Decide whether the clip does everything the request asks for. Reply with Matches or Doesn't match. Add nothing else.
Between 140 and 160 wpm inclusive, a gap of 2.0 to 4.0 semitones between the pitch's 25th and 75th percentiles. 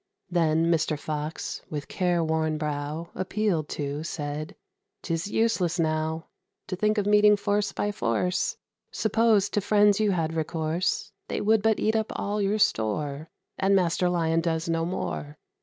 Doesn't match